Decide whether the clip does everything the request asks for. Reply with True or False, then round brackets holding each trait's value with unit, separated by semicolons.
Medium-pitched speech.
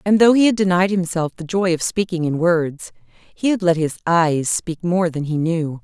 True (170 Hz)